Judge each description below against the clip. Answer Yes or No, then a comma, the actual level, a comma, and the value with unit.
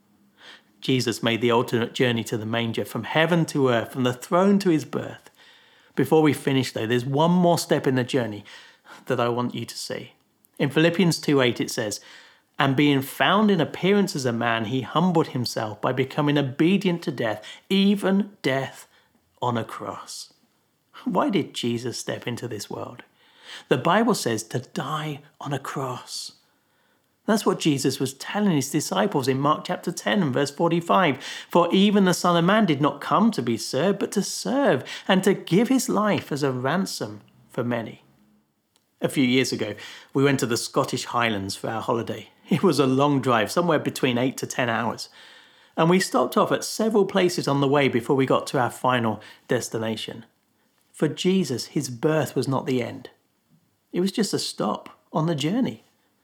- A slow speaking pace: No, average, 185 wpm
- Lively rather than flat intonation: Yes, wide, 6.1 semitones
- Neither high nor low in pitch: Yes, medium, 145 Hz